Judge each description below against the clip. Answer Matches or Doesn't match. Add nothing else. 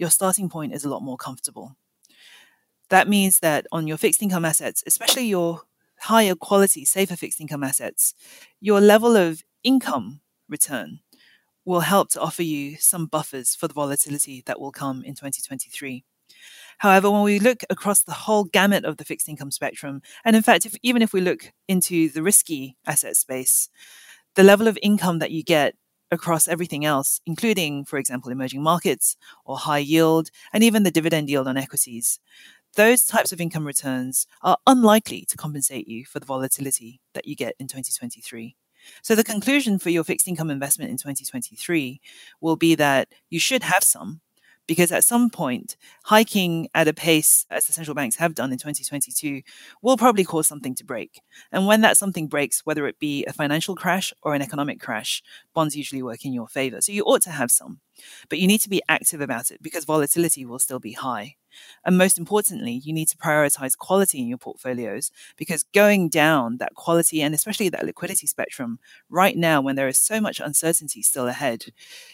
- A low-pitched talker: Doesn't match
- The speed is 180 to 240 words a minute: Matches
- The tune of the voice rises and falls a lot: Matches